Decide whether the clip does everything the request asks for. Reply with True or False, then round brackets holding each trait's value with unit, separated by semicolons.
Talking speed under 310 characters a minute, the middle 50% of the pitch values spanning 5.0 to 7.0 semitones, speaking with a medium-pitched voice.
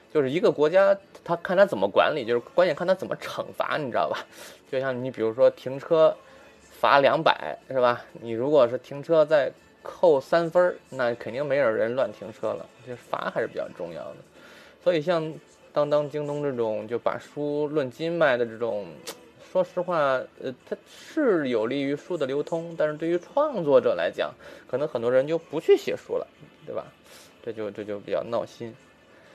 True (270 characters per minute; 5.5 semitones; 155 Hz)